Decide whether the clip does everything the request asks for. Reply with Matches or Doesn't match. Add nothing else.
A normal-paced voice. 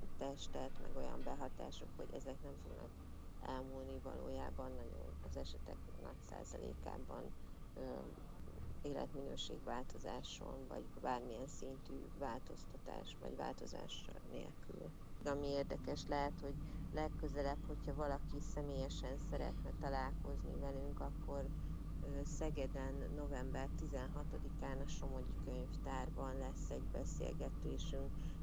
Doesn't match